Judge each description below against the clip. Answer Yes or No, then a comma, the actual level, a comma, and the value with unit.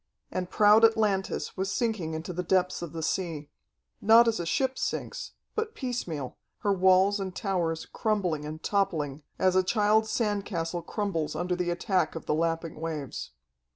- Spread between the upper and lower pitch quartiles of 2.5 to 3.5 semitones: No, average, 4.1 semitones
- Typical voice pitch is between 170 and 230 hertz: Yes, medium, 185 Hz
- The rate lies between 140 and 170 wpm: Yes, average, 165 wpm